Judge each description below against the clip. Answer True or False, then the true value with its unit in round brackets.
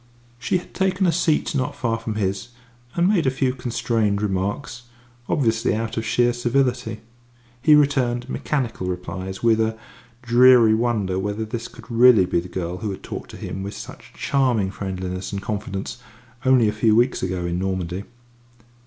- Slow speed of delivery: False (170 wpm)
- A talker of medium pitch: False (115 Hz)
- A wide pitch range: False (4.5 semitones)